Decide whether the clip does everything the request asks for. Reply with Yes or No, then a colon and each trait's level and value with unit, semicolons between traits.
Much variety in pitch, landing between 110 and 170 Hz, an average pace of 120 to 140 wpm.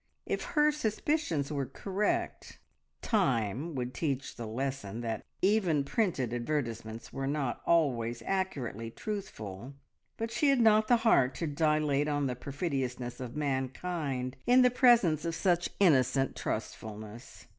Yes: wide, 7.3 semitones; medium, 140 Hz; slow, 135 wpm